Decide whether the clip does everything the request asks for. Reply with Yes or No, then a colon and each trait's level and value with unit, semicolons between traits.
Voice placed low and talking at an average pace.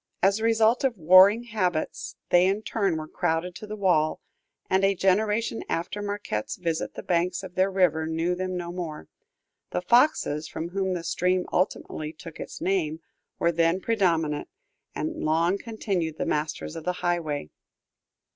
No: medium, 180 Hz; average, 165 wpm